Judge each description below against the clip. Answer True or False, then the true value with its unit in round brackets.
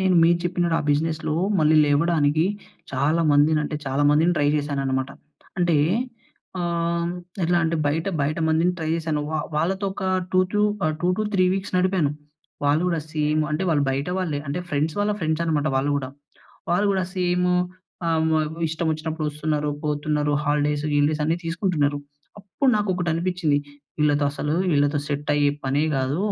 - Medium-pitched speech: True (155 Hz)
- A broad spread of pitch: False (2.8 semitones)